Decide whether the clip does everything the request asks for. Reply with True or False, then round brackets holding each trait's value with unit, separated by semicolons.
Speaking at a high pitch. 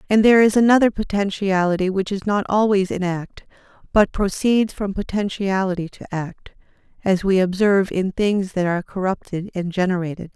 True (195 Hz)